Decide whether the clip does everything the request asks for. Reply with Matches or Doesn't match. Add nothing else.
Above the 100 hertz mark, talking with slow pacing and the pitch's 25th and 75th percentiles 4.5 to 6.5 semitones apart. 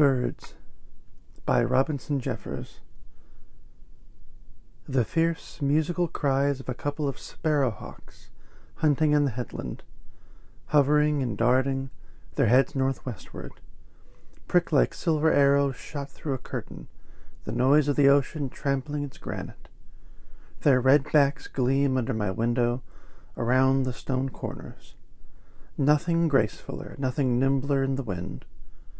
Doesn't match